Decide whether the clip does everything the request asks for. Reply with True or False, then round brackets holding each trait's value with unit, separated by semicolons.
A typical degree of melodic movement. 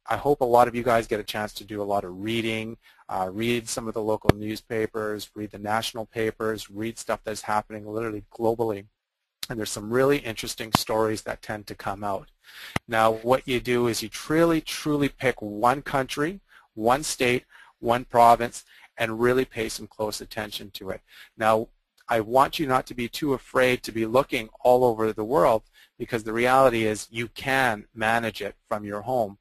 False (2.3 semitones)